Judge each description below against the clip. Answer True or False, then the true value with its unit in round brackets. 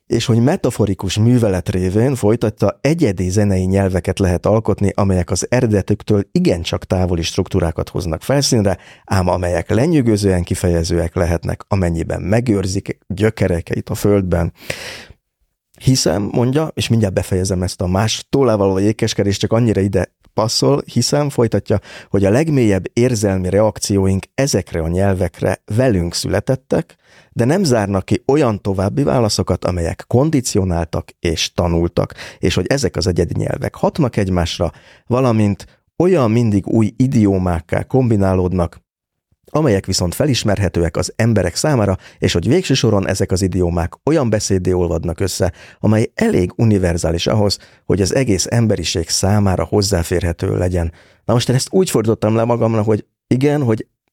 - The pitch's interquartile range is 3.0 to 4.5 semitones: True (4.0 semitones)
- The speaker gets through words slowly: False (130 wpm)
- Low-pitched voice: True (100 Hz)